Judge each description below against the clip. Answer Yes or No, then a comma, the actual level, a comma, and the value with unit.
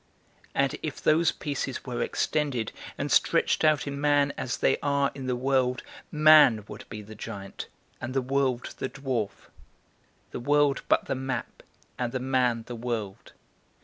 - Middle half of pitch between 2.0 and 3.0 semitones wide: Yes, average, 2.7 semitones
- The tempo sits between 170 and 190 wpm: No, average, 160 wpm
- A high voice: No, low, 130 Hz